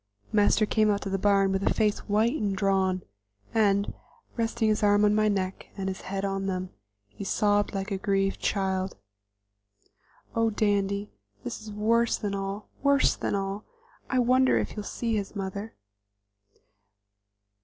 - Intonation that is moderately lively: No, narrow, 1.7 semitones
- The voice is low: No, high, 205 Hz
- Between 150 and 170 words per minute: Yes, average, 160 wpm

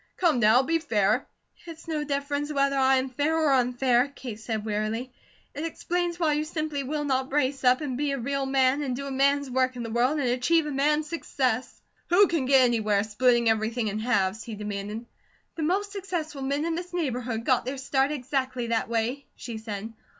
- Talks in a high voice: Yes, very high, 265 Hz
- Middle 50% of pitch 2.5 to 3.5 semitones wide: No, average, 3.9 semitones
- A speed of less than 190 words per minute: No, average, 200 wpm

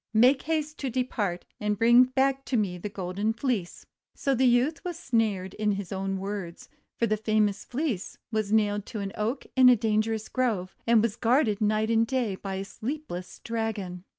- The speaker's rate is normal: Yes, average, 185 wpm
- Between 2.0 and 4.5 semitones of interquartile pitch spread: Yes, average, 3.8 semitones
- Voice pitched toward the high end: Yes, high, 220 Hz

